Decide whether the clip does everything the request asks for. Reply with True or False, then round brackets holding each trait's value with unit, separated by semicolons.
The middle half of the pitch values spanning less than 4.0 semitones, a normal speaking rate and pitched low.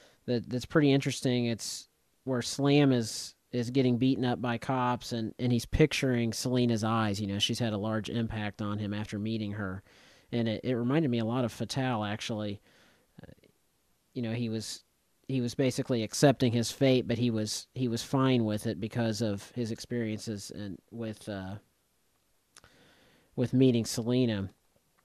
True (2.7 semitones; 170 wpm; 115 Hz)